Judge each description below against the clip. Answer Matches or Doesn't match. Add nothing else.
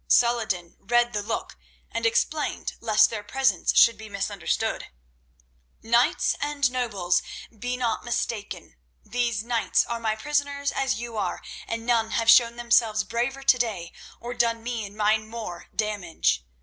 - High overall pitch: Matches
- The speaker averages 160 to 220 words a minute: Doesn't match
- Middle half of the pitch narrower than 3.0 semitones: Matches